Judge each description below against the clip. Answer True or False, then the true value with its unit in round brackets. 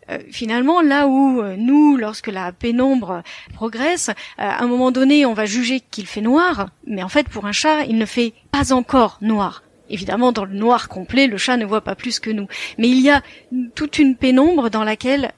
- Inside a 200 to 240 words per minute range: True (215 wpm)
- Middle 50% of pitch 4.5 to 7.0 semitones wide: False (4.1 semitones)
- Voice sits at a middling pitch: False (245 Hz)